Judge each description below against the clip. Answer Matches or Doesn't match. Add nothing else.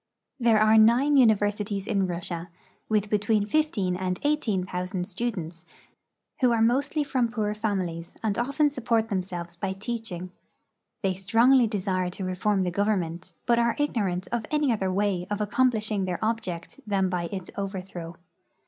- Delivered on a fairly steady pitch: Doesn't match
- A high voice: Matches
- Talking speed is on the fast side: Doesn't match